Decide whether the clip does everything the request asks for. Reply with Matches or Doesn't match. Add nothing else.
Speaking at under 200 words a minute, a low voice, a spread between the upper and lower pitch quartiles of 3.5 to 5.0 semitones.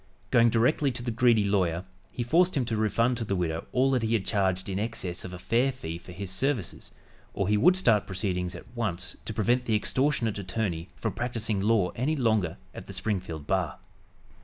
Doesn't match